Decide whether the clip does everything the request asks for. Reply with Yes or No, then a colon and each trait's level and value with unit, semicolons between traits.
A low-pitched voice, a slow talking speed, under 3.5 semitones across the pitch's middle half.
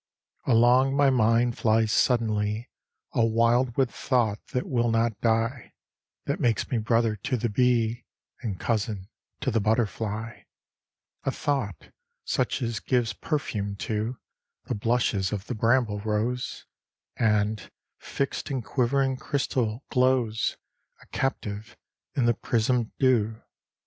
Yes: low, 115 Hz; slow, 125 wpm; narrow, 2.6 semitones